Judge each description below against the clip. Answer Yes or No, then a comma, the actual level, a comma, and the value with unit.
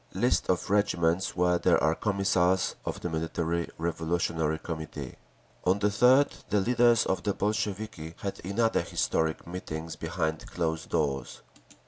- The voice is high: No, very low, 90 Hz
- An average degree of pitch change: Yes, average, 3.9 semitones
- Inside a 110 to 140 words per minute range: Yes, slow, 135 wpm